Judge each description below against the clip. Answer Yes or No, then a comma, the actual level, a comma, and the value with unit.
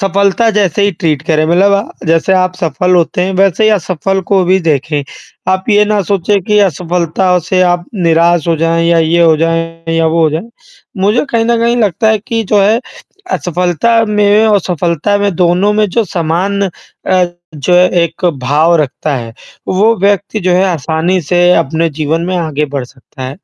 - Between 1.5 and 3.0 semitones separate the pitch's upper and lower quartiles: No, average, 3.5 semitones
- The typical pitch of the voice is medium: Yes, medium, 180 Hz